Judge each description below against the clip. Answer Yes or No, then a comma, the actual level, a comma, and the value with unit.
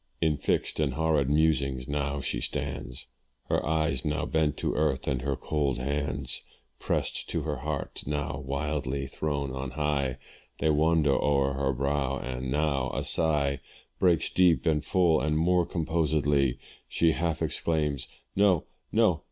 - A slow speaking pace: No, average, 150 wpm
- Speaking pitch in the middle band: No, very low, 75 Hz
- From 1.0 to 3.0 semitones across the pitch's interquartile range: Yes, narrow, 2.4 semitones